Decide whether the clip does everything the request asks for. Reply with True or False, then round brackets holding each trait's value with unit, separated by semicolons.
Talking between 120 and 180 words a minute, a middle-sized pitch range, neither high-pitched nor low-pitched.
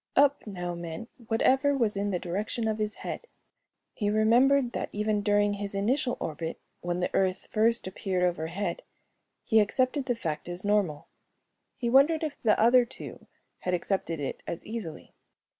False (160 wpm; 4.8 semitones; 210 Hz)